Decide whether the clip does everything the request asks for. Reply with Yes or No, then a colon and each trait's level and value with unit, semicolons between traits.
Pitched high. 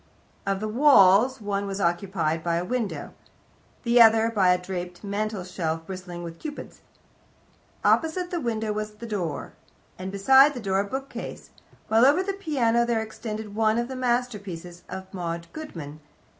Yes: high, 210 Hz